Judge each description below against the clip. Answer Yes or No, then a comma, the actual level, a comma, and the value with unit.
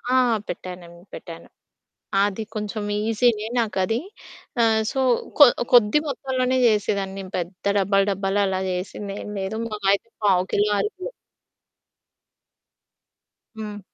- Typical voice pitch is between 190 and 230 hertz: Yes, high, 205 Hz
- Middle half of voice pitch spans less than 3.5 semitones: Yes, narrow, 2.4 semitones